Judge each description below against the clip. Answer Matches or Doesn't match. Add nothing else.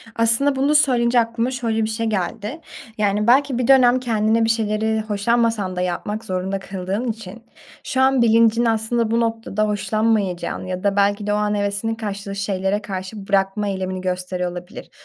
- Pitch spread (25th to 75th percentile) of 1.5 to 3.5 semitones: Matches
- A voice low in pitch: Doesn't match